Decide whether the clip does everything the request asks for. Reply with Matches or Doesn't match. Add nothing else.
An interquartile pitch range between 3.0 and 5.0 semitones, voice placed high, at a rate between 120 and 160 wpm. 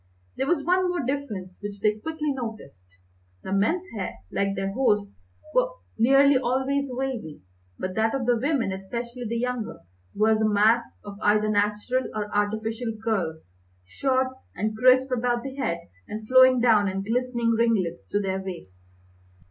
Matches